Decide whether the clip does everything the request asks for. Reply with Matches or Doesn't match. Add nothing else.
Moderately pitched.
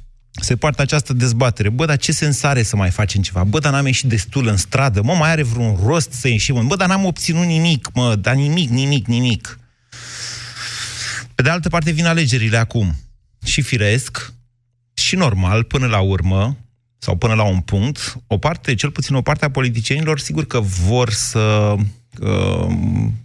Doesn't match